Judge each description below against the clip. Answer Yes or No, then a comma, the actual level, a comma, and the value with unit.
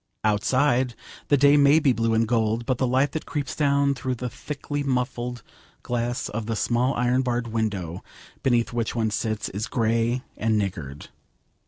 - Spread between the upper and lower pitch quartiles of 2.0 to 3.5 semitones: Yes, average, 2.8 semitones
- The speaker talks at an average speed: Yes, average, 170 wpm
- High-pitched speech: No, low, 120 Hz